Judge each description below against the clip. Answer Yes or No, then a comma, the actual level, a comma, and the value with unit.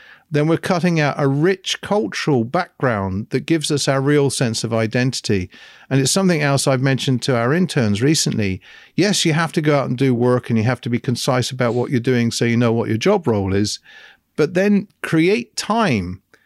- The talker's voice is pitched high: No, low, 135 Hz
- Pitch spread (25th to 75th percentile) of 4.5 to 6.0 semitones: Yes, average, 5.2 semitones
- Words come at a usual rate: No, fast, 210 wpm